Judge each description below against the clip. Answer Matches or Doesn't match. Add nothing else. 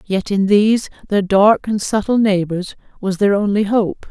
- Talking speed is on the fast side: Doesn't match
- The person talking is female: Matches